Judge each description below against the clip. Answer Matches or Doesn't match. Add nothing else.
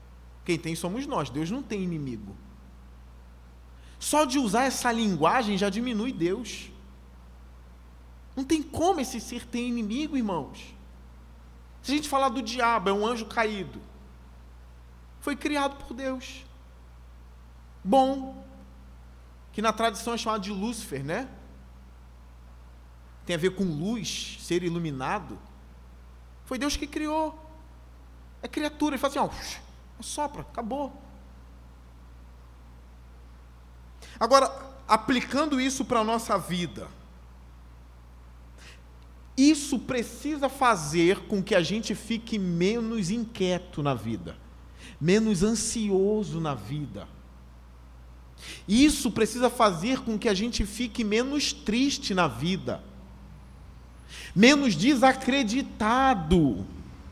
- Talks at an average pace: Doesn't match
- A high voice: Doesn't match